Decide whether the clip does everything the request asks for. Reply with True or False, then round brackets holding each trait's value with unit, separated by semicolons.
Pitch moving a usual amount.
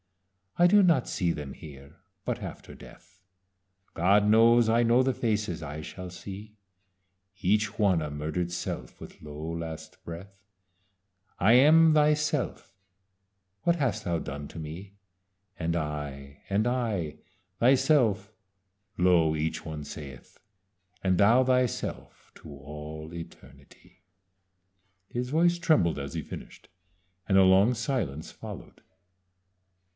False (7.4 semitones)